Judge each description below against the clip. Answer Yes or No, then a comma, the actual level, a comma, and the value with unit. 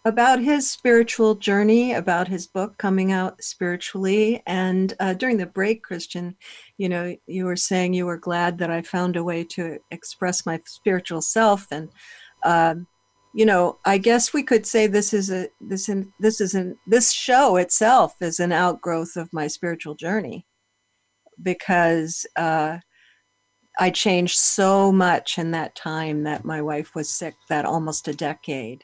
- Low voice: No, medium, 180 Hz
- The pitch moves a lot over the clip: No, average, 3.6 semitones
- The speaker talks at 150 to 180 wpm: Yes, average, 165 wpm